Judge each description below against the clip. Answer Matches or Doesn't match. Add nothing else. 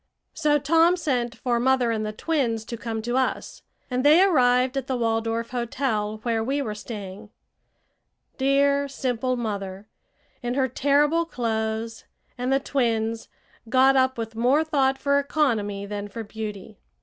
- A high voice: Matches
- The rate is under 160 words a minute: Matches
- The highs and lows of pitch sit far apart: Doesn't match